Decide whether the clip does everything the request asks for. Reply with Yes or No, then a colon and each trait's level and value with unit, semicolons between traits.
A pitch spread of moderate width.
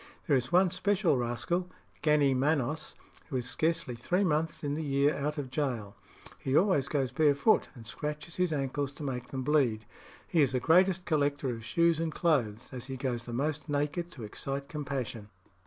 Yes: average, 3.8 semitones